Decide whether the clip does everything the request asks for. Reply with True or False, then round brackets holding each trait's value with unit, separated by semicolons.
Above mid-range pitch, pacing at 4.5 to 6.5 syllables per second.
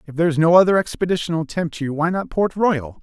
False (165 Hz; 5.5 syllables/s)